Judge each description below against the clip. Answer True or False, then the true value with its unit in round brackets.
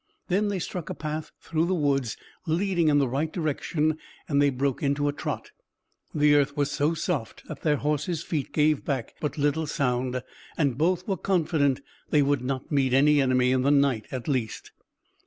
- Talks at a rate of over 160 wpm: True (190 wpm)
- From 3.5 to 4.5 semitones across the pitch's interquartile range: False (2.6 semitones)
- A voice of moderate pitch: True (145 Hz)